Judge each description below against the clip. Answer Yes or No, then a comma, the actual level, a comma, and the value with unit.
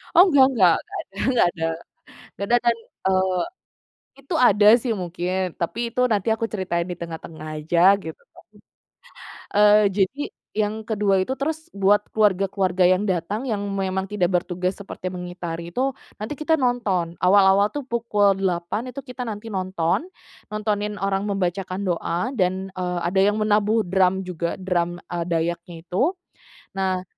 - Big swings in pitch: No, average, 2.9 semitones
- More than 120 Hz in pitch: Yes, high, 190 Hz